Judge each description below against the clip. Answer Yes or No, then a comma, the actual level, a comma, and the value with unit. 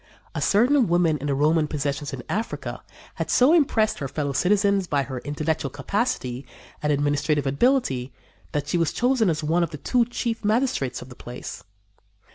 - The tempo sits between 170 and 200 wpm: Yes, average, 175 wpm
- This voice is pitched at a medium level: Yes, medium, 155 Hz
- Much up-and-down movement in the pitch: Yes, wide, 7.4 semitones